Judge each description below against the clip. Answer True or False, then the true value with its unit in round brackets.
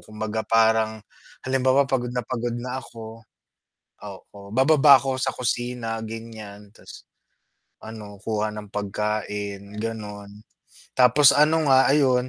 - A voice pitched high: False (115 Hz)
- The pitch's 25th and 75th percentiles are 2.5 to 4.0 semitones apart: True (3.5 semitones)